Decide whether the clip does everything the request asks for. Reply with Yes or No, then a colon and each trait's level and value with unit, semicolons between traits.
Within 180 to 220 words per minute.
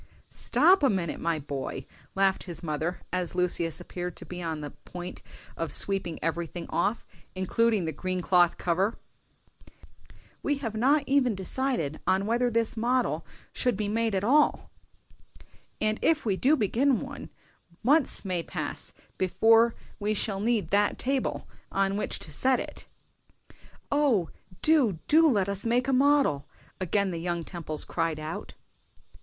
No: average, 150 wpm